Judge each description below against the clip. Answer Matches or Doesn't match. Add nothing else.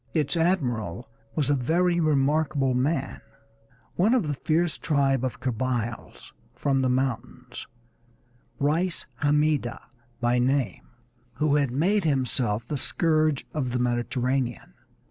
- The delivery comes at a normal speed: Doesn't match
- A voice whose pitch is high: Doesn't match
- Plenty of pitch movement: Doesn't match